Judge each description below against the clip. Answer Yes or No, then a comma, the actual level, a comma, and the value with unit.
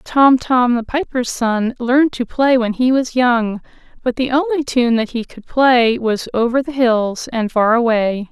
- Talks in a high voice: Yes, high, 245 Hz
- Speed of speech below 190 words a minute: No, average, 195 wpm